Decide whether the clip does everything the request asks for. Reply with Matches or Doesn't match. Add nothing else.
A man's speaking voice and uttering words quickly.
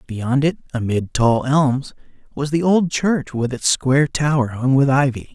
Doesn't match